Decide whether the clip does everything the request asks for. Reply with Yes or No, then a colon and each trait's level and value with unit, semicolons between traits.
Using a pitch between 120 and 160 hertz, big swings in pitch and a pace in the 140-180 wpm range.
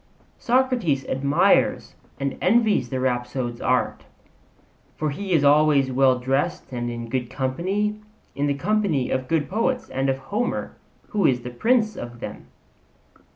Yes: medium, 140 Hz; wide, 7.7 semitones; average, 145 wpm